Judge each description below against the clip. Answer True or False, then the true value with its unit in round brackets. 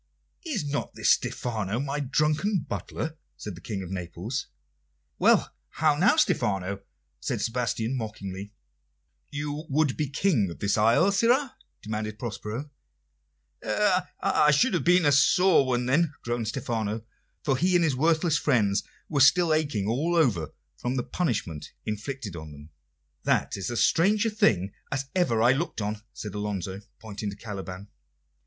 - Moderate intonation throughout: False (7.1 semitones)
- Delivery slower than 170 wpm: True (150 wpm)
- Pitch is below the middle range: True (125 Hz)